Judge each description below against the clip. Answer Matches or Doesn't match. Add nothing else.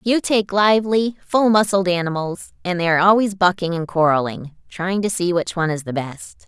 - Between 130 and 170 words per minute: Doesn't match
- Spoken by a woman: Matches